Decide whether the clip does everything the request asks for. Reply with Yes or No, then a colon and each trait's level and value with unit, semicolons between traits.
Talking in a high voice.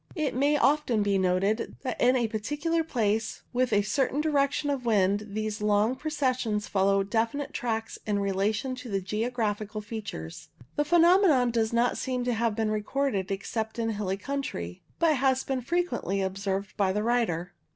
Yes: high, 225 Hz